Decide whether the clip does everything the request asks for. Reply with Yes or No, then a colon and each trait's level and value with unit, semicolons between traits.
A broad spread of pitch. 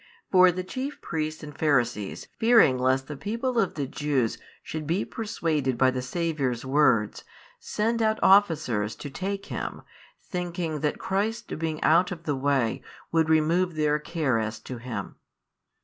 Yes: wide, 5.7 semitones